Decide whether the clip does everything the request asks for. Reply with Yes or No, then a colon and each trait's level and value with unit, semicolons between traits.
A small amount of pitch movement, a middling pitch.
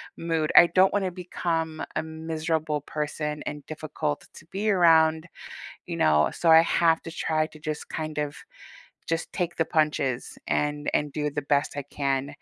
Yes: narrow, 1.8 semitones; medium, 155 Hz